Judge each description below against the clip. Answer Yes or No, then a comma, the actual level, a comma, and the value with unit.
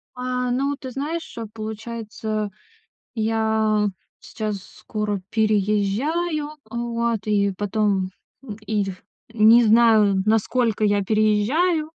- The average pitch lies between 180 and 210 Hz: No, high, 220 Hz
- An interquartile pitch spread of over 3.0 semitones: No, narrow, 2.5 semitones